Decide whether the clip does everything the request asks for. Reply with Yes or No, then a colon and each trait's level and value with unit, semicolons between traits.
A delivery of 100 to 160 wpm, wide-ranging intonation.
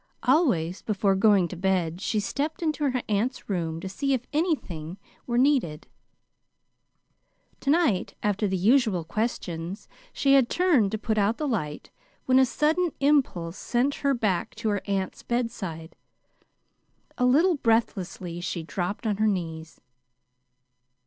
Yes: average, 140 wpm; wide, 6.7 semitones